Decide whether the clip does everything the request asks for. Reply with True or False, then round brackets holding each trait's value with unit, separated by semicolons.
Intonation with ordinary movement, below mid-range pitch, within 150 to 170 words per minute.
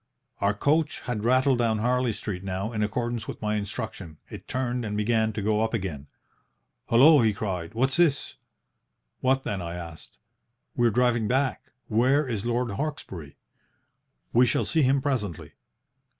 True (3.7 semitones; 115 Hz; 160 wpm)